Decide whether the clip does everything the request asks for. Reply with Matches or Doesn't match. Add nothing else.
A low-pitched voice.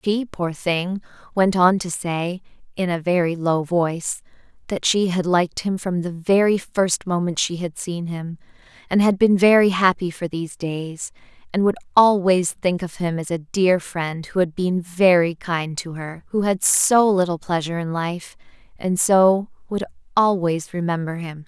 Doesn't match